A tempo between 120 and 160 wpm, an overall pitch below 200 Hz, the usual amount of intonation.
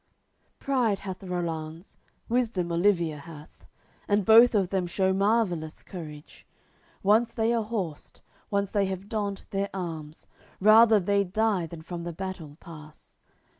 Yes: average, 140 wpm; high, 190 Hz; average, 3.8 semitones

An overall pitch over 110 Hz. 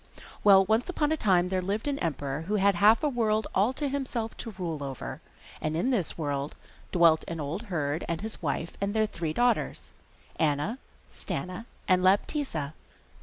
Yes: high, 190 Hz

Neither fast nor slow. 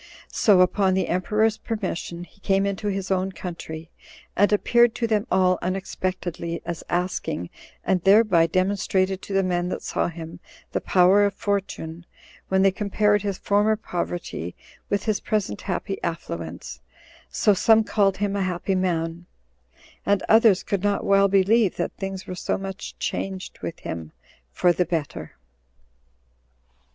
Yes: average, 150 wpm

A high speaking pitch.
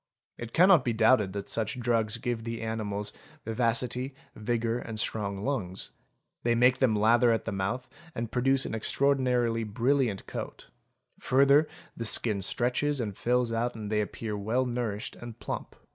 No: low, 115 Hz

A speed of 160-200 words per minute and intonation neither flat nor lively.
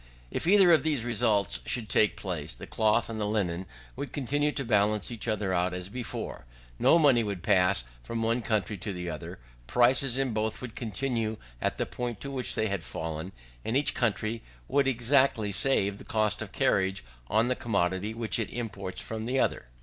Yes: average, 190 wpm; average, 4.0 semitones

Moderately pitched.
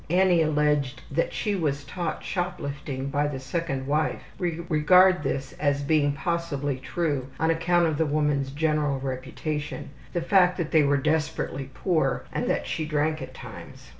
Yes: medium, 150 Hz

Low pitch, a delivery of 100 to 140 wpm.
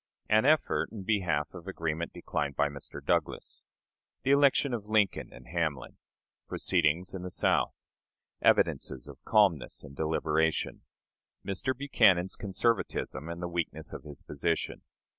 Yes: very low, 90 Hz; slow, 135 wpm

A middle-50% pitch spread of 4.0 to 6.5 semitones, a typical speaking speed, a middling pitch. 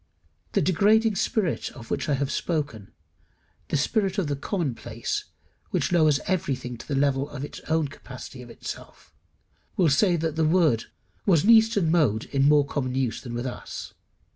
Yes: average, 4.8 semitones; average, 170 wpm; medium, 150 Hz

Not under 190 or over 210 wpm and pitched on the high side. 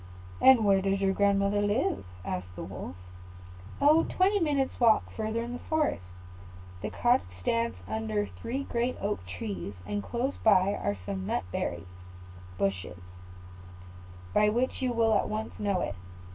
No: average, 150 wpm; high, 205 Hz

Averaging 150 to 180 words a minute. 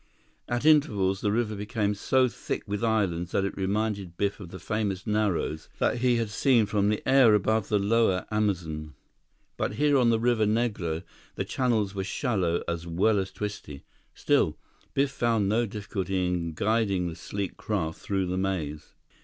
Yes: average, 170 wpm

